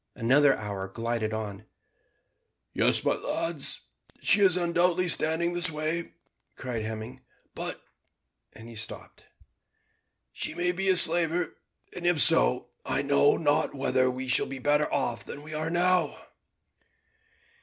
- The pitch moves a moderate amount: No, wide, 6.5 semitones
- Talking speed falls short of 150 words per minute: Yes, average, 140 wpm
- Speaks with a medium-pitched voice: Yes, medium, 150 Hz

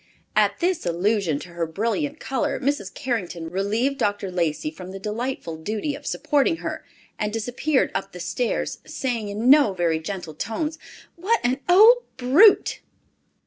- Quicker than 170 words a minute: No, average, 150 wpm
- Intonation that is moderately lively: No, wide, 7.5 semitones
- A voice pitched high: Yes, high, 220 Hz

